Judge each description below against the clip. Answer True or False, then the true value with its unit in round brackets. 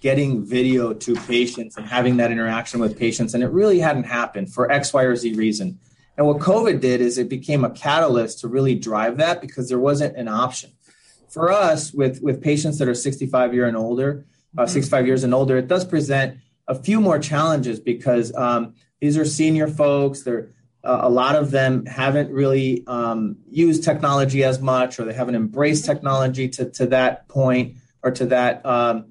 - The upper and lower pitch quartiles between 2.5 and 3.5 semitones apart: True (2.8 semitones)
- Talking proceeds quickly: False (195 wpm)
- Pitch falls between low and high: False (130 Hz)